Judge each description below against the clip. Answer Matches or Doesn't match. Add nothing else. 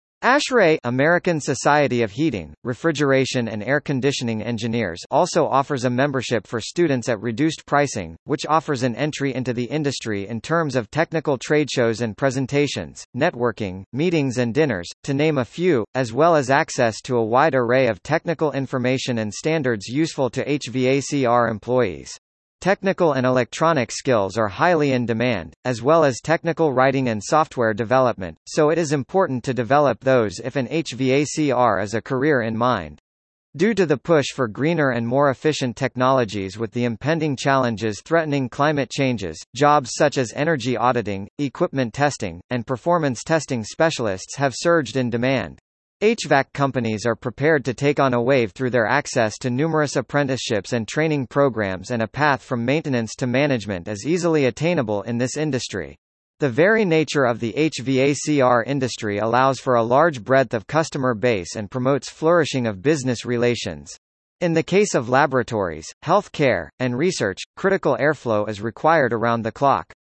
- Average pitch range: Matches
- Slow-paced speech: Doesn't match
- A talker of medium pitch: Doesn't match